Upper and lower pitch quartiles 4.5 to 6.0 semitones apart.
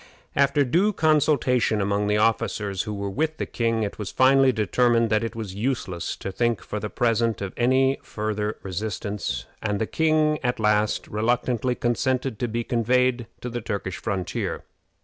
No: average, 3.5 semitones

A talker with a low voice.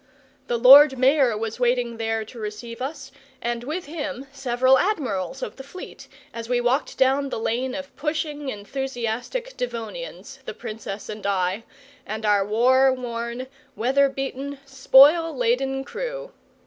No: very high, 255 Hz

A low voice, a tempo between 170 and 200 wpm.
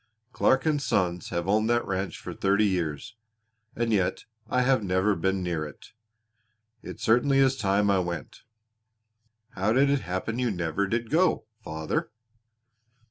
No: low, 100 Hz; average, 150 wpm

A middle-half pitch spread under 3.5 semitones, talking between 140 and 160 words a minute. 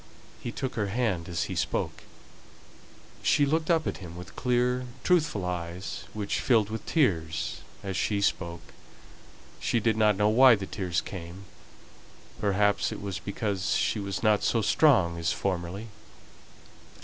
No: average, 4.4 semitones; average, 150 wpm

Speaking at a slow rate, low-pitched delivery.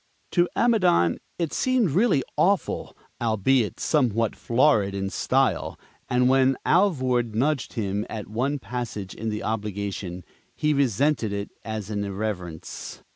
Yes: slow, 130 wpm; low, 115 Hz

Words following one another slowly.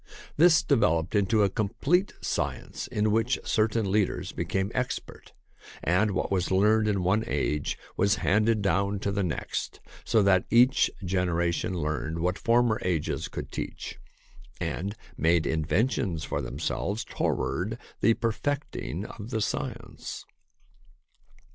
Yes: slow, 130 wpm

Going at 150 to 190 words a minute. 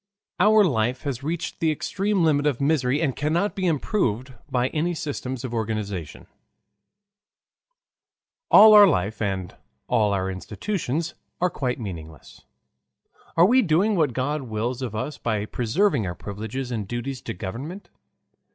No: average, 140 wpm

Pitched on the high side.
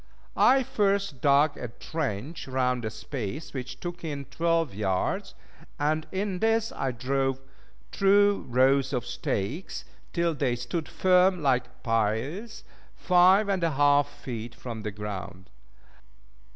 No: medium, 140 Hz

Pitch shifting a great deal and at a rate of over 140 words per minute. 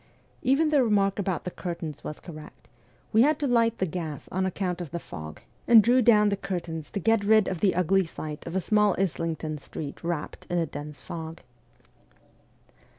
No: average, 4.6 semitones; average, 190 wpm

